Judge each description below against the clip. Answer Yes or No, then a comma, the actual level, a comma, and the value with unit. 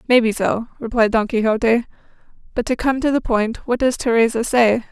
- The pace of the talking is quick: No, average, 195 wpm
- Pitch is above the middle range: Yes, high, 235 Hz